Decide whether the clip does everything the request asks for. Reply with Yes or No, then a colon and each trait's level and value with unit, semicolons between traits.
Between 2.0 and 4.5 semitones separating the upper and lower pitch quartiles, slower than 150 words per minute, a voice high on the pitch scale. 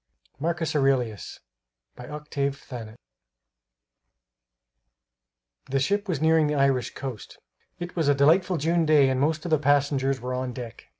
No: average, 3.3 semitones; average, 140 wpm; medium, 140 Hz